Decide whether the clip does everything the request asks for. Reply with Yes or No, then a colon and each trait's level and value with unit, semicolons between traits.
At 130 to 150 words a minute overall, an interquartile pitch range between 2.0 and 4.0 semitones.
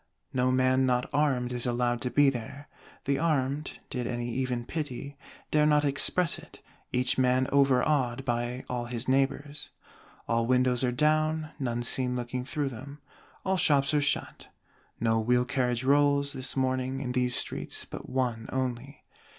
No: average, 160 wpm; narrow, 2.4 semitones